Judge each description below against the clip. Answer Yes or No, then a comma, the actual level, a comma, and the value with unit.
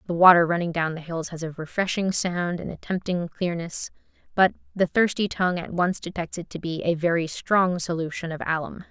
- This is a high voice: No, medium, 175 Hz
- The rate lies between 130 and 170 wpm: No, average, 200 wpm